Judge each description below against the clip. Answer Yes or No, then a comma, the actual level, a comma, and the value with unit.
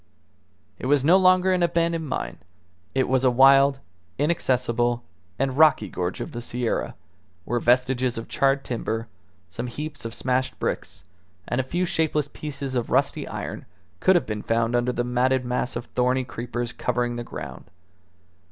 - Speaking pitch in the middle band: No, low, 125 Hz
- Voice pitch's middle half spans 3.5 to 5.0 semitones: No, average, 3.0 semitones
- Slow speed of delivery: No, average, 160 wpm